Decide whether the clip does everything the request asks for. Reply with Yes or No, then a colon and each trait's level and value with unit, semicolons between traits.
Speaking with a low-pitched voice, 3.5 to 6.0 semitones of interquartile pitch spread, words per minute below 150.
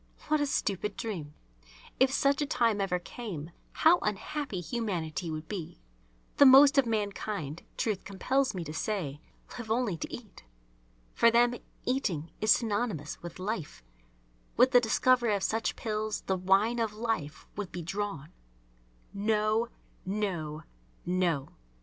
No: high, 210 Hz; average, 5.2 semitones; average, 140 wpm